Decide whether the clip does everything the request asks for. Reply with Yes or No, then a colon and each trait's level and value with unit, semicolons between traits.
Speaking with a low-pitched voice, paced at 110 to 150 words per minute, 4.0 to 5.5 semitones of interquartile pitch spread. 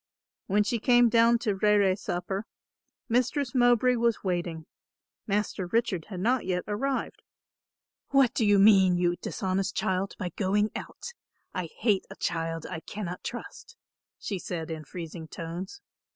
No: high, 200 Hz; average, 140 wpm; average, 4.6 semitones